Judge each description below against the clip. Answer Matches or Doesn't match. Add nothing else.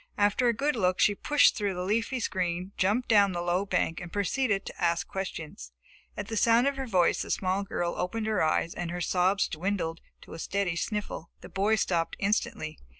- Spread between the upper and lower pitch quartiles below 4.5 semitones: Matches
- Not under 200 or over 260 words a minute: Matches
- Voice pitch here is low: Doesn't match